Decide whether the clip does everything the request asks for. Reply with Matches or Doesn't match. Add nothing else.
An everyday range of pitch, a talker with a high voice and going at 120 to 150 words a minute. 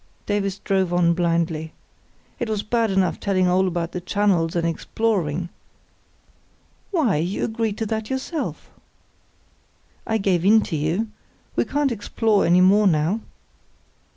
Matches